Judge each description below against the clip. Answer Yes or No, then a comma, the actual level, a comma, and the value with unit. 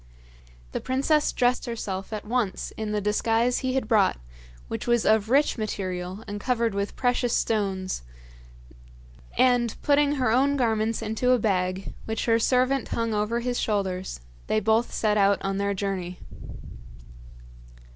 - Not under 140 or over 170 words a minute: Yes, average, 145 wpm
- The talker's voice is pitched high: Yes, high, 220 Hz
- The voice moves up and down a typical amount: Yes, average, 3.6 semitones